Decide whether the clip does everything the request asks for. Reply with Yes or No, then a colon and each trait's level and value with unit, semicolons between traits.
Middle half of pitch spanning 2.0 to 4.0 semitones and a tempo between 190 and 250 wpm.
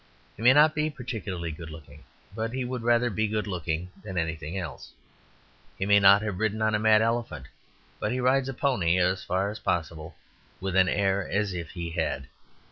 No: average, 4.7 semitones; average, 200 wpm